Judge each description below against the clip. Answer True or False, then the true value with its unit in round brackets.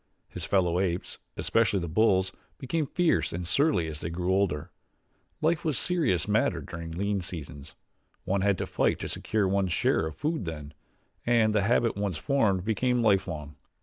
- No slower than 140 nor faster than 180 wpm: True (175 wpm)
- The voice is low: True (95 Hz)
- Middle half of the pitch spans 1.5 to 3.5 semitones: False (5.1 semitones)